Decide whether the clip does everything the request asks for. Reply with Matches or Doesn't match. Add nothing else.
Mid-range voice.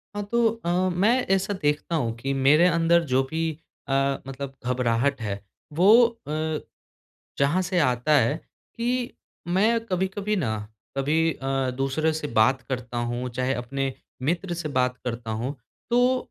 Matches